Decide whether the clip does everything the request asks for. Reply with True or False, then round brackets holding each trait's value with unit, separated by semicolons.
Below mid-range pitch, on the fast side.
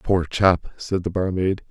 False (90 Hz; 175 wpm)